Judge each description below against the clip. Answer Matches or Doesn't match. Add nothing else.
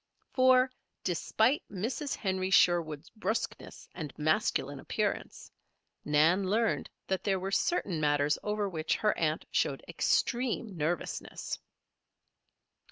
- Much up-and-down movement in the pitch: Matches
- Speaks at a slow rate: Matches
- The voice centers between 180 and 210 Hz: Matches